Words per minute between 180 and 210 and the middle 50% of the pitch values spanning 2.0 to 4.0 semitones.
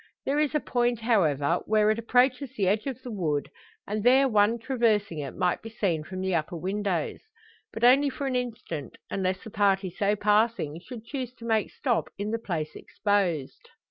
No: average, 190 wpm; average, 4.6 semitones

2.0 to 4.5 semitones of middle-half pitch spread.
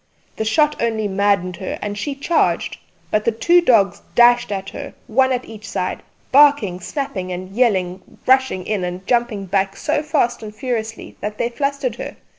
No: average, 5.1 semitones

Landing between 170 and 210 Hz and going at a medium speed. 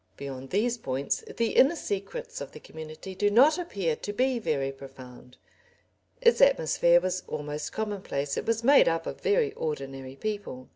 Yes: medium, 185 Hz; average, 160 wpm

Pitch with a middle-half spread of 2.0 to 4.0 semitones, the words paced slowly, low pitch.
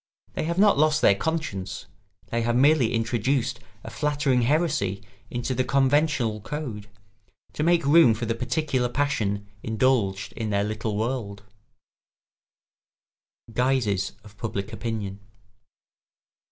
No: average, 5.3 semitones; slow, 125 wpm; low, 120 Hz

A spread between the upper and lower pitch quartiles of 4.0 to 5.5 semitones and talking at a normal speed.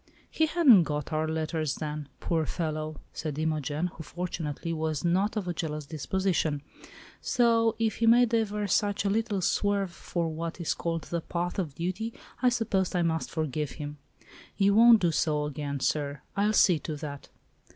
Yes: average, 4.8 semitones; average, 170 wpm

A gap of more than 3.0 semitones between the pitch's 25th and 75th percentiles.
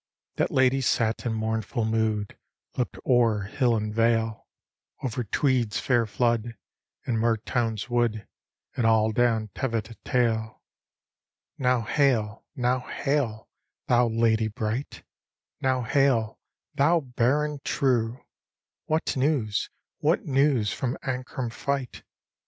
No: average, 2.7 semitones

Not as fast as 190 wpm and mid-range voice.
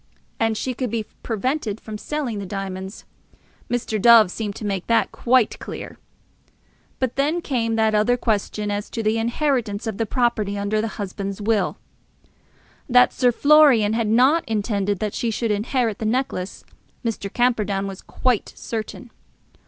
No: average, 160 wpm; high, 225 Hz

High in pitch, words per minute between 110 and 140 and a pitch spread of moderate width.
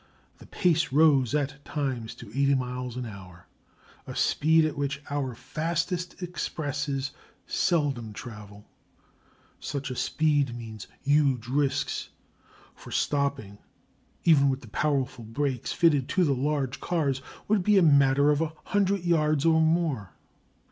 No: medium, 140 Hz; slow, 135 wpm; average, 3.7 semitones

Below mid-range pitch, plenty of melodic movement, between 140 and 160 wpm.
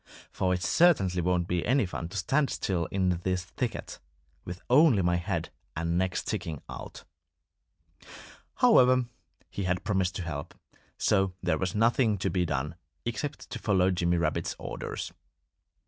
No: very low, 90 Hz; average, 3.2 semitones; average, 150 wpm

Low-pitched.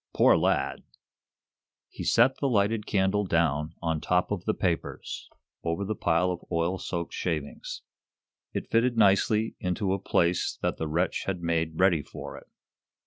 Yes: very low, 90 Hz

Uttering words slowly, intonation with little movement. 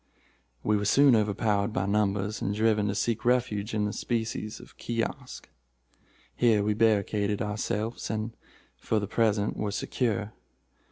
No: average, 145 wpm; narrow, 1.7 semitones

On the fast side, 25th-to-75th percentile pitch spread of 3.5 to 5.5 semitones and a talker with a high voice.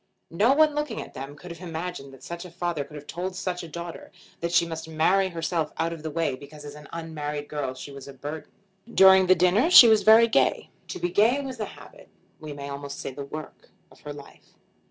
No: fast, 235 wpm; average, 4.0 semitones; medium, 165 Hz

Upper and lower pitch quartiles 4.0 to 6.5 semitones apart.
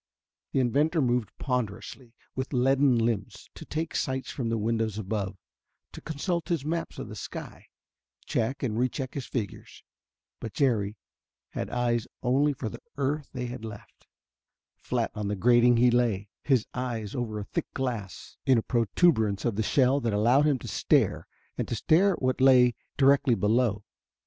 No: average, 3.4 semitones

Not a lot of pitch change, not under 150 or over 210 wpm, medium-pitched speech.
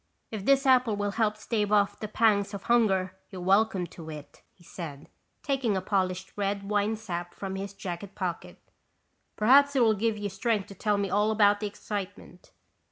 No: narrow, 2.3 semitones; average, 180 wpm; high, 205 Hz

